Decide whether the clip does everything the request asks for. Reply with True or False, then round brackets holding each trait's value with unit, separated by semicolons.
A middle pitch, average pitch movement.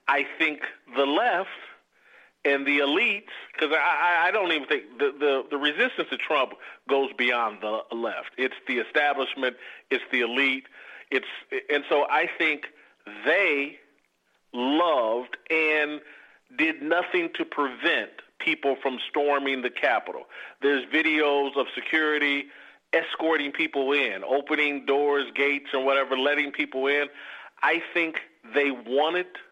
False (145 Hz; 2.0 semitones)